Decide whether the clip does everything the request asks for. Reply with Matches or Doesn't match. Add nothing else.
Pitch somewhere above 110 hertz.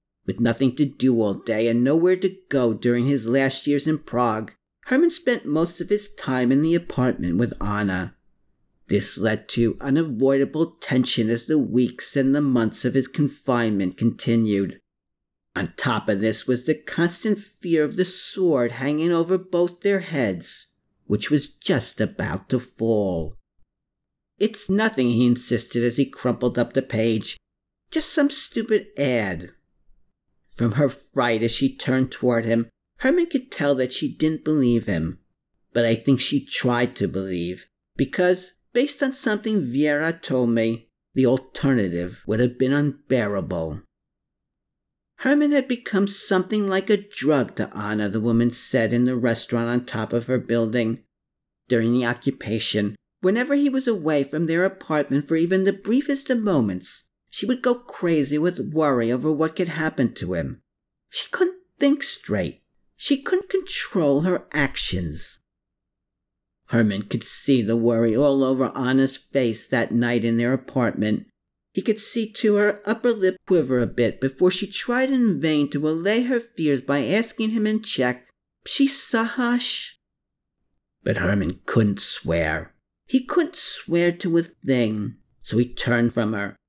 Matches